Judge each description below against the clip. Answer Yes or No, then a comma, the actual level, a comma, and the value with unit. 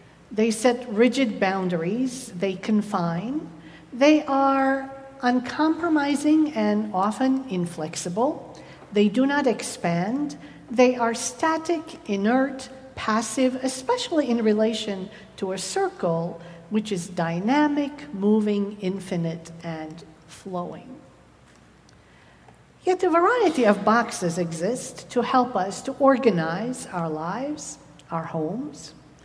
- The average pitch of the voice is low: No, high, 225 Hz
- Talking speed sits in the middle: No, slow, 100 wpm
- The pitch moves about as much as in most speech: No, wide, 6.4 semitones